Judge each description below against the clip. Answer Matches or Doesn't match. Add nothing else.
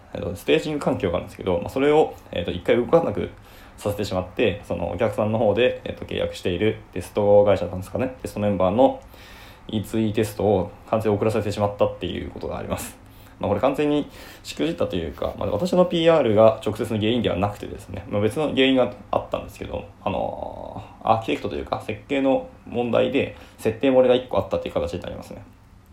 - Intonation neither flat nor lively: Matches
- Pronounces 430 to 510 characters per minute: Matches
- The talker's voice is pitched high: Doesn't match